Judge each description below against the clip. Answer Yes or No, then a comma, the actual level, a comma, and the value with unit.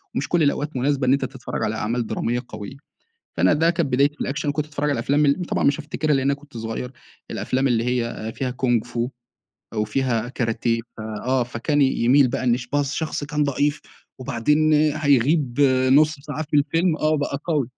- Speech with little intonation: No, average, 3.3 semitones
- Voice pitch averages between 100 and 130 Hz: No, medium, 140 Hz